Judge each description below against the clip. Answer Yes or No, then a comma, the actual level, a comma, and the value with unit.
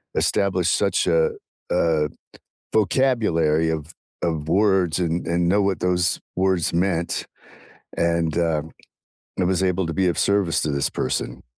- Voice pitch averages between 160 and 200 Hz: No, very low, 85 Hz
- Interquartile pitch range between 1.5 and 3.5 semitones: Yes, average, 2.7 semitones